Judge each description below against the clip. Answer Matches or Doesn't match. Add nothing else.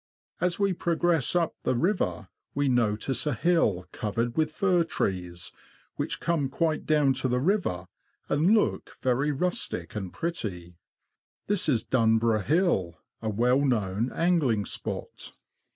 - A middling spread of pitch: Doesn't match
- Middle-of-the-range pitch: Doesn't match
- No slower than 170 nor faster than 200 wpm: Doesn't match